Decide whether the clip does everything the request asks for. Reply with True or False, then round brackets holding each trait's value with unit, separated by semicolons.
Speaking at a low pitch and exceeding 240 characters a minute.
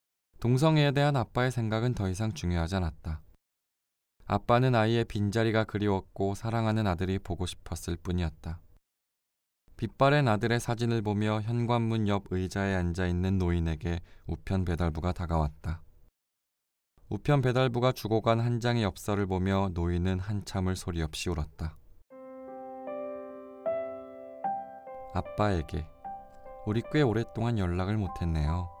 True (95 Hz; 285 characters per minute)